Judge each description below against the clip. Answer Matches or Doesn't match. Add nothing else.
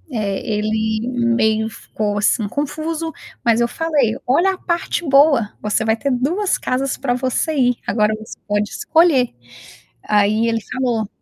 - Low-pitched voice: Doesn't match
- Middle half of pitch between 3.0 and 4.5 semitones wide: Doesn't match